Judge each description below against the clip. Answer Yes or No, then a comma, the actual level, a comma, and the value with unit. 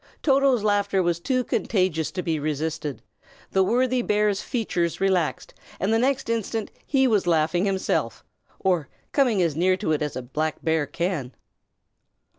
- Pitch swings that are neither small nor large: No, wide, 5.7 semitones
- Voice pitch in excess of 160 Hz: Yes, medium, 185 Hz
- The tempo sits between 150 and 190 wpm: Yes, average, 155 wpm